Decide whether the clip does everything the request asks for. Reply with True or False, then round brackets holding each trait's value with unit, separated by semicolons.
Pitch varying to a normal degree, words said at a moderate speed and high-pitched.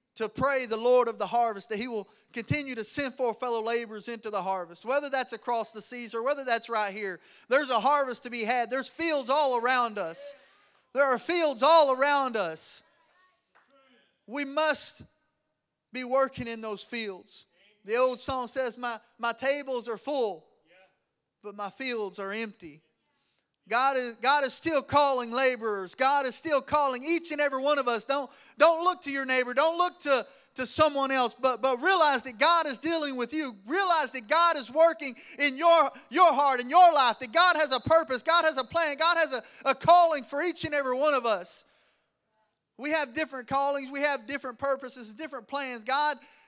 True (4.0 semitones; 190 wpm; 265 Hz)